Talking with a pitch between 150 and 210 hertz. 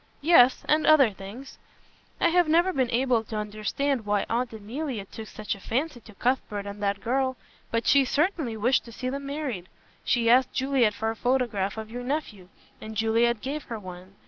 No: high, 240 Hz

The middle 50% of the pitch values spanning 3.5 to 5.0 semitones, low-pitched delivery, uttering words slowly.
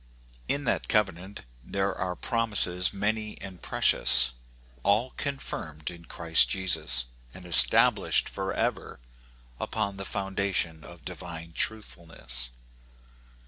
Yes: average, 3.9 semitones; very low, 95 Hz; slow, 105 wpm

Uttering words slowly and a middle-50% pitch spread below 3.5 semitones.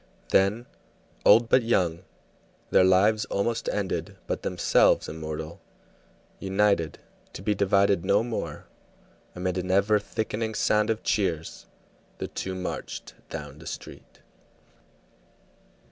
Yes: slow, 115 wpm; average, 3.0 semitones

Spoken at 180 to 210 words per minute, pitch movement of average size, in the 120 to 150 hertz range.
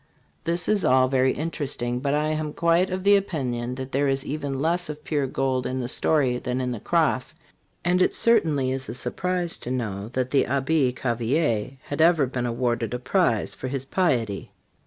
Yes: average, 195 wpm; average, 4.3 semitones; low, 135 Hz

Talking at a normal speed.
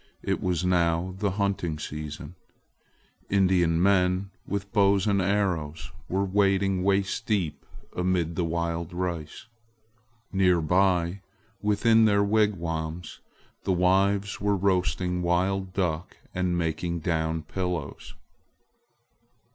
No: slow, 105 wpm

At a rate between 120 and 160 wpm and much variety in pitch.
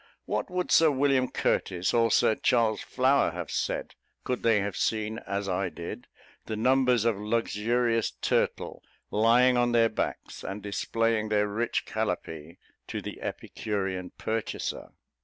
No: average, 140 wpm; average, 3.0 semitones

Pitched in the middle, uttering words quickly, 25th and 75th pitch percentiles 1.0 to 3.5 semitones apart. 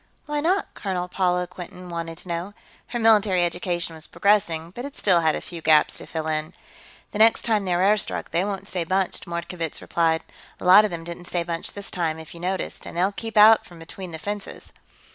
Yes: medium, 180 Hz; fast, 220 wpm; average, 3.2 semitones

